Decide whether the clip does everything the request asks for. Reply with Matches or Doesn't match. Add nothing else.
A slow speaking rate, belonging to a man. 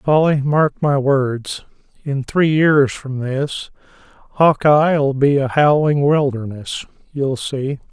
Matches